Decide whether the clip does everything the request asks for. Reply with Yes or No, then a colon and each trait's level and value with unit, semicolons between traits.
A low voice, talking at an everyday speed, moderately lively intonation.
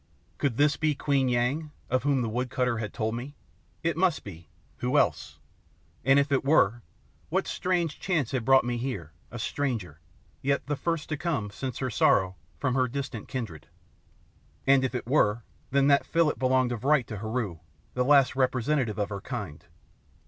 Yes: low, 130 Hz; average, 180 wpm; average, 3.8 semitones